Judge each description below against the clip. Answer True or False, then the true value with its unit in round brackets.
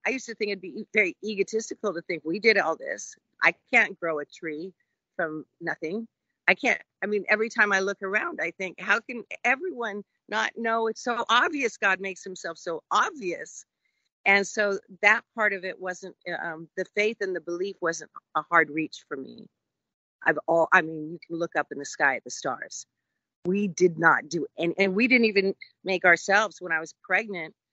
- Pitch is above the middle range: True (195 Hz)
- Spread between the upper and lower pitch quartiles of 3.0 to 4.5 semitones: True (4.0 semitones)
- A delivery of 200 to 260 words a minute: True (205 wpm)